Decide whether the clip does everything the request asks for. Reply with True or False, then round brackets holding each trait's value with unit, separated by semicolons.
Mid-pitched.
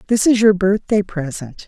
False (195 Hz)